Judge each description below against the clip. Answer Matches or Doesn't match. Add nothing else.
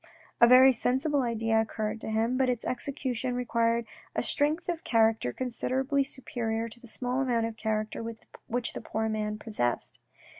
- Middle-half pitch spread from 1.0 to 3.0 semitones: Matches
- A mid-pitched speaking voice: Doesn't match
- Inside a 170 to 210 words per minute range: Doesn't match